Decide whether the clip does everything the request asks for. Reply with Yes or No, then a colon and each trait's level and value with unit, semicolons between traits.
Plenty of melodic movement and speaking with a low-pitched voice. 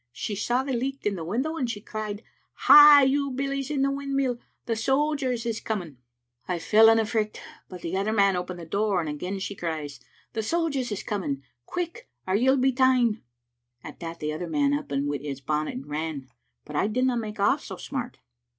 No: wide, 7.1 semitones; high, 220 Hz